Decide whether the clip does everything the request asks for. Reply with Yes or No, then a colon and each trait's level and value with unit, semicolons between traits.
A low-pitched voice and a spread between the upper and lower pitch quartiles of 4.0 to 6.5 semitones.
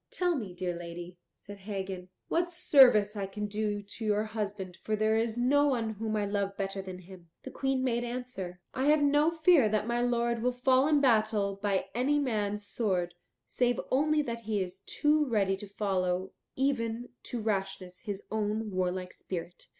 No: high, 215 Hz; average, 4.3 semitones